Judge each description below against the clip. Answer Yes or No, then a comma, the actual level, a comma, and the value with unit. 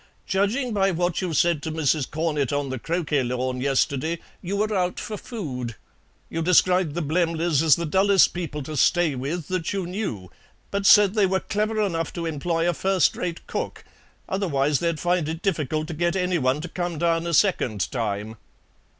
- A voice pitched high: No, medium, 170 Hz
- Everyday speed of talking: Yes, average, 185 wpm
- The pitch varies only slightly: No, average, 4.1 semitones